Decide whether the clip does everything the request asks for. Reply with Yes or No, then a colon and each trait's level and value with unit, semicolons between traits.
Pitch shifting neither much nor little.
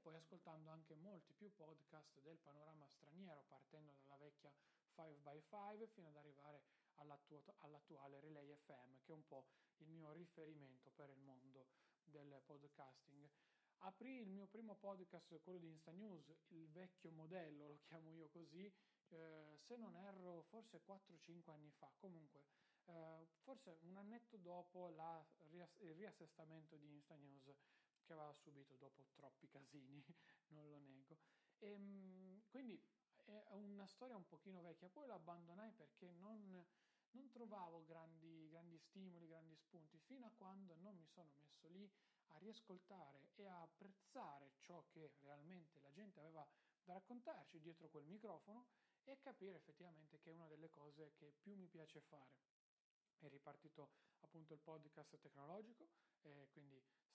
Yes: average, 4.3 semitones